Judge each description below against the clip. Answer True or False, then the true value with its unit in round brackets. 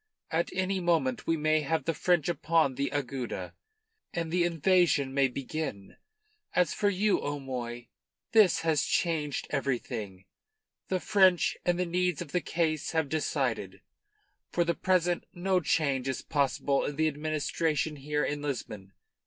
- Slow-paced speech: False (145 wpm)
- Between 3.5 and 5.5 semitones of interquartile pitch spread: True (4.1 semitones)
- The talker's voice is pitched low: False (155 Hz)